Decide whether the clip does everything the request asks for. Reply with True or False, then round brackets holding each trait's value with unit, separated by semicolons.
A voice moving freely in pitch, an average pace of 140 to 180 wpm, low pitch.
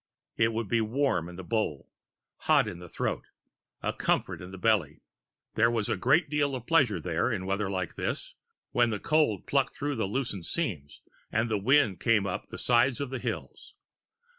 False (5.7 semitones; 190 wpm; 110 Hz)